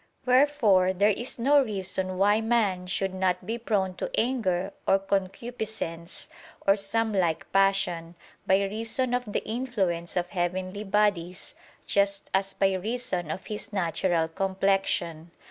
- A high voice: Yes, high, 195 Hz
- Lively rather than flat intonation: No, average, 3.1 semitones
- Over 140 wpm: No, slow, 135 wpm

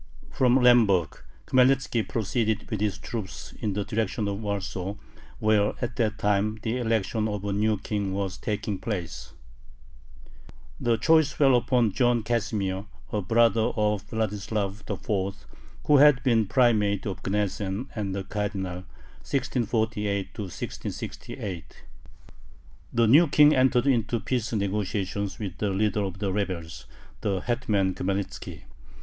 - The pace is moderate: No, slow, 130 wpm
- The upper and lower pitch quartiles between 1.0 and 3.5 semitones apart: Yes, average, 3.1 semitones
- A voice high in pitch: No, low, 105 Hz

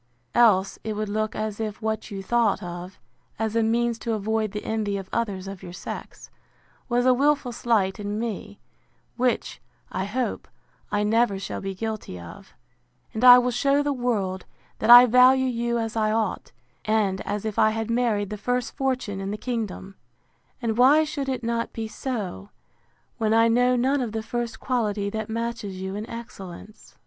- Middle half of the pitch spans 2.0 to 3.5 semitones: Yes, average, 2.8 semitones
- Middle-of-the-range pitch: No, high, 220 Hz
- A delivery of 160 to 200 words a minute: Yes, average, 180 wpm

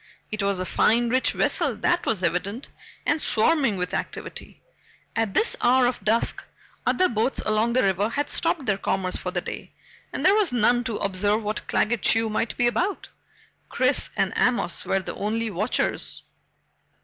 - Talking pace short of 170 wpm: No, average, 175 wpm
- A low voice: No, high, 225 Hz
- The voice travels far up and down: No, average, 3.7 semitones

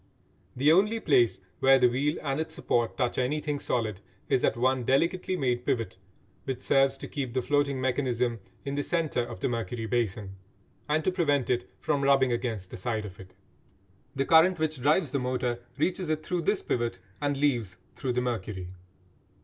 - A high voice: No, low, 130 Hz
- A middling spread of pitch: Yes, average, 3.7 semitones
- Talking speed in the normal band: Yes, average, 180 wpm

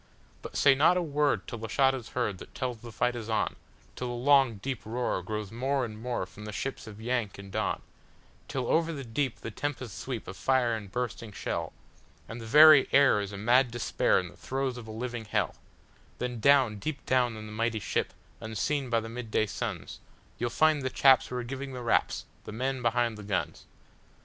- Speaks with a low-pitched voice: Yes, low, 120 Hz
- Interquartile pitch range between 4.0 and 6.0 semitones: No, average, 3.4 semitones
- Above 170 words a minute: Yes, average, 200 wpm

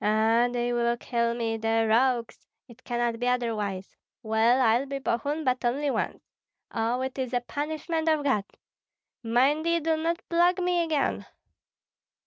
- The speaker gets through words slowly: No, average, 155 wpm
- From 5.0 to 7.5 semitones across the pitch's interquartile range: No, average, 4.2 semitones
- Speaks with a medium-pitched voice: No, high, 245 Hz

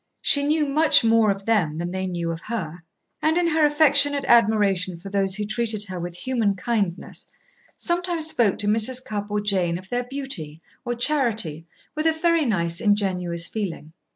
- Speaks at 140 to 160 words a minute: No, average, 180 wpm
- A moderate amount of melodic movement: No, wide, 6.9 semitones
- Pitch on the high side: Yes, high, 215 Hz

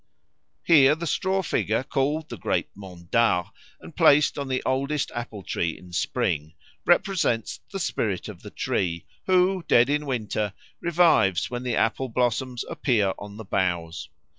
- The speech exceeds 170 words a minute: No, average, 155 wpm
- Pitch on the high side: No, low, 120 Hz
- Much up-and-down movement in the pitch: Yes, wide, 7.3 semitones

